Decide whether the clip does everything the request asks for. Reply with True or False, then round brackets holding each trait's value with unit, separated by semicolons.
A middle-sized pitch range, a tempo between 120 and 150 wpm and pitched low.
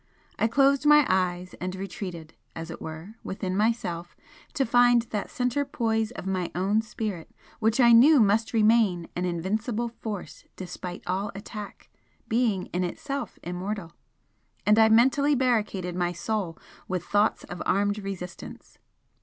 False (4.2 semitones; 145 wpm; 210 Hz)